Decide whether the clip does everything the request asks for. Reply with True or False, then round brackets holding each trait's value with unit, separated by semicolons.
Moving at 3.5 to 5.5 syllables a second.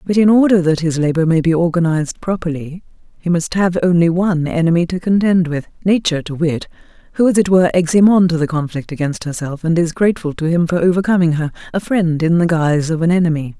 False (6.2 syllables/s)